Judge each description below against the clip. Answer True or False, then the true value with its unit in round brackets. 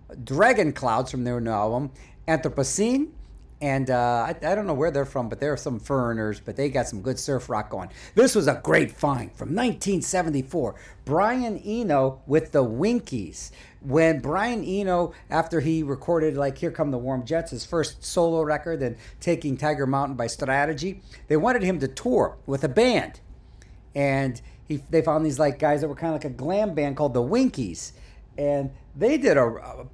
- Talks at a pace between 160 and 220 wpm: True (190 wpm)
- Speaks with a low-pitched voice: False (145 Hz)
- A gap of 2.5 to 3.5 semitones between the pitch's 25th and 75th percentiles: False (4.0 semitones)